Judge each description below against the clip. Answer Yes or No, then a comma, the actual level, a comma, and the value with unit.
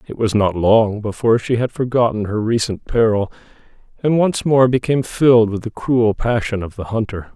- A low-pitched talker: Yes, low, 115 Hz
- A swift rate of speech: No, average, 190 wpm